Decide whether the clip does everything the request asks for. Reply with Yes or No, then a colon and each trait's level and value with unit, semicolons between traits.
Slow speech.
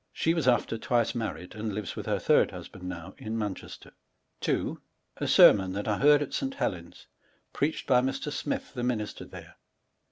No: average, 185 wpm